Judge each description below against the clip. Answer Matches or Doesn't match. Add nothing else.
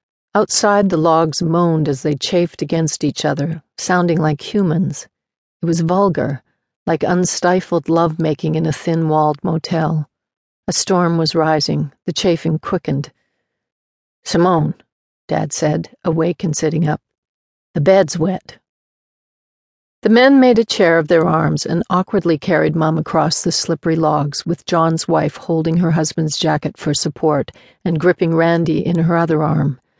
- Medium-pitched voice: Matches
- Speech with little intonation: Matches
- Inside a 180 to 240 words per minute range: Doesn't match